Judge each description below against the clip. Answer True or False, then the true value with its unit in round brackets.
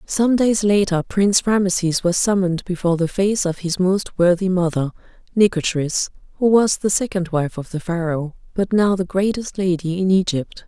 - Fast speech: False (175 wpm)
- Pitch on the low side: False (185 Hz)